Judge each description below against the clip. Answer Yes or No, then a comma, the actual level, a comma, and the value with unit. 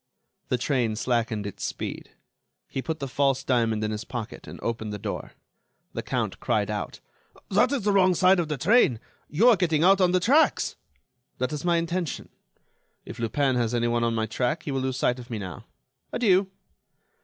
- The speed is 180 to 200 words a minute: Yes, average, 190 wpm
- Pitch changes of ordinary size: No, wide, 7.4 semitones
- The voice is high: No, low, 135 Hz